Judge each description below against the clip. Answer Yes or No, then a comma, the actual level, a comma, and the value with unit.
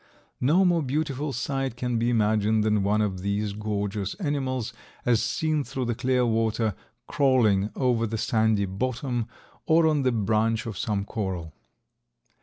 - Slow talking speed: No, average, 150 wpm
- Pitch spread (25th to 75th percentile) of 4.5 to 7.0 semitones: No, average, 3.7 semitones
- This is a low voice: Yes, low, 115 Hz